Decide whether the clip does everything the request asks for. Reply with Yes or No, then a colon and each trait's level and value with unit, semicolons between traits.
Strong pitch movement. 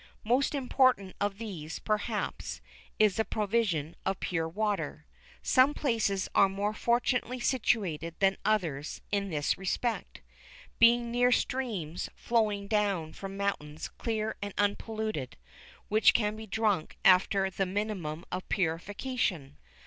No: average, 3.5 semitones